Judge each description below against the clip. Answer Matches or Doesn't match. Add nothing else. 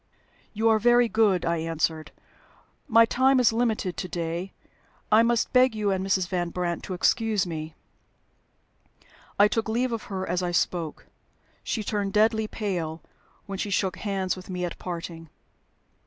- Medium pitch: Doesn't match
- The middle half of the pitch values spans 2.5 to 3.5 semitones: Doesn't match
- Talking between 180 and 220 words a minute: Doesn't match